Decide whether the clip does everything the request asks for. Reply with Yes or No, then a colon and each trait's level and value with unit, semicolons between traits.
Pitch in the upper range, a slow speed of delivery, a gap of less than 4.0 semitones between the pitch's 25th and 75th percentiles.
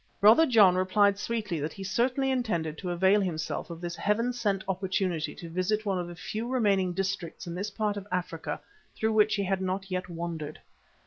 No: high, 195 Hz; average, 195 wpm; average, 3.1 semitones